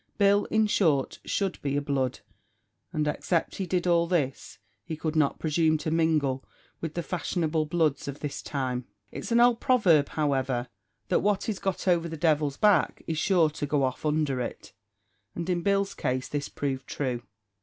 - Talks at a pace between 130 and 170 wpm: No, average, 180 wpm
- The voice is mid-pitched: Yes, medium, 155 Hz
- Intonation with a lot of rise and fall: No, average, 4.0 semitones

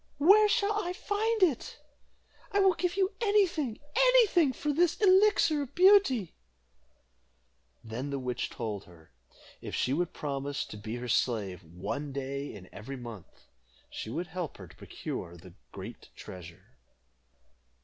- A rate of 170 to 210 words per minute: No, average, 150 wpm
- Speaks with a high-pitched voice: No, medium, 170 Hz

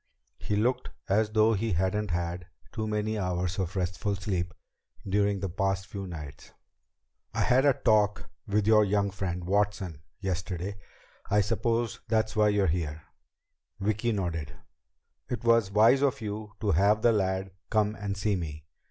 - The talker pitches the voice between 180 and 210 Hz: No, low, 100 Hz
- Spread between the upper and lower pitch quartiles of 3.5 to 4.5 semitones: No, average, 2.7 semitones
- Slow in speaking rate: No, average, 155 wpm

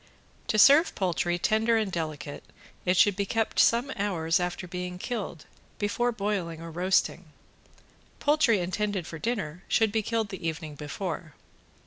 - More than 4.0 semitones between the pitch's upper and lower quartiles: Yes, average, 4.5 semitones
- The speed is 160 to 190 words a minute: No, average, 145 wpm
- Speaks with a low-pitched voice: No, high, 190 Hz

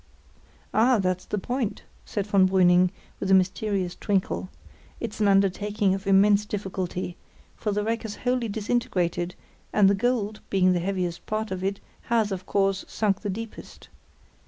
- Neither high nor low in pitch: No, high, 200 Hz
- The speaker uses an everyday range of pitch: No, narrow, 2.3 semitones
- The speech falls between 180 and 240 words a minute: No, average, 160 wpm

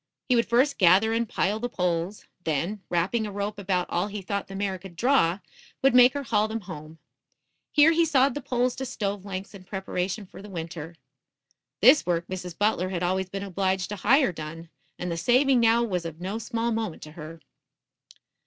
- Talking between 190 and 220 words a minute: Yes, average, 200 wpm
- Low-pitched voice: No, high, 195 Hz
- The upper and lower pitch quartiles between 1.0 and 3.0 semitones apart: No, average, 4.6 semitones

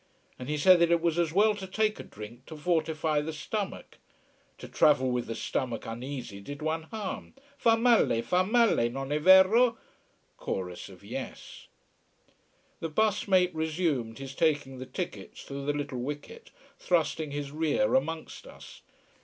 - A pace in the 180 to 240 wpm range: No, average, 160 wpm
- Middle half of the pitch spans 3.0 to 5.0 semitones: No, wide, 5.5 semitones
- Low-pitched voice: No, medium, 155 Hz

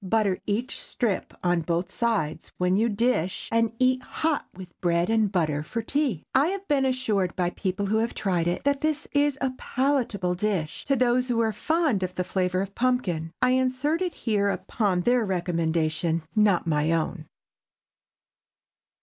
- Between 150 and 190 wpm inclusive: Yes, average, 165 wpm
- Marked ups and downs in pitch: Yes, wide, 6.2 semitones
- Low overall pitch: No, high, 205 Hz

